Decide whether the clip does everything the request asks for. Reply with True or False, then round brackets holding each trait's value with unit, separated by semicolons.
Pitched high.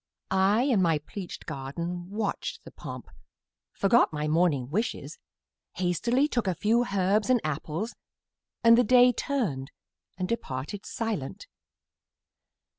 True (195 Hz)